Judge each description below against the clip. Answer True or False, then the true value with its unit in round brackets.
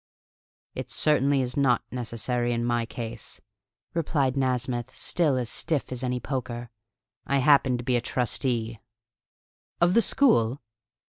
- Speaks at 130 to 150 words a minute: True (135 wpm)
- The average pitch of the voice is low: True (125 Hz)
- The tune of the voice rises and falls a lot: False (2.6 semitones)